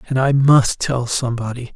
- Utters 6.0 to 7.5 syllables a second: No, 5.2 syllables/s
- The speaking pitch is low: Yes, low, 125 Hz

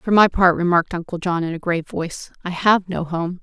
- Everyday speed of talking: No, fast, 245 wpm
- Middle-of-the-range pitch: Yes, medium, 175 Hz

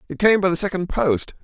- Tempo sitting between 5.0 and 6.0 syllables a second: Yes, 5.9 syllables/s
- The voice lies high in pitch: No, medium, 175 Hz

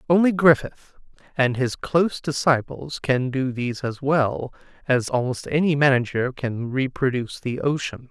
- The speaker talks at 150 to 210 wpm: No, average, 140 wpm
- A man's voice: Yes, male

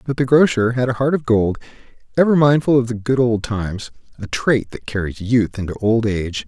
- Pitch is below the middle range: Yes, low, 120 Hz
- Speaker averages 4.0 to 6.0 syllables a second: Yes, 5.5 syllables/s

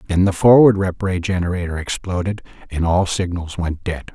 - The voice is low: Yes, very low, 90 Hz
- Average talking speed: Yes, average, 175 wpm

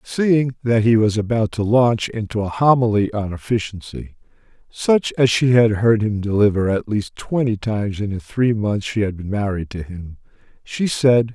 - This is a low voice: Yes, low, 110 Hz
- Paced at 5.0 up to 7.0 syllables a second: No, 4.6 syllables/s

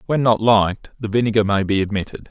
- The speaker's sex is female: No, male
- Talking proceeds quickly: Yes, fast, 210 wpm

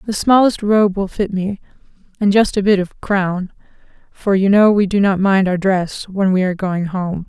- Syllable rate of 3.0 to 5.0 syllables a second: Yes, 4.7 syllables/s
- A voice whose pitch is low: No, high, 195 Hz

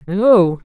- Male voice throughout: No, female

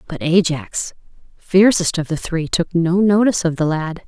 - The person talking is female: Yes, female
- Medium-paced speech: Yes, average, 175 wpm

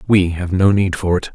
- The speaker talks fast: Yes, fast, 270 wpm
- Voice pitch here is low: Yes, very low, 95 Hz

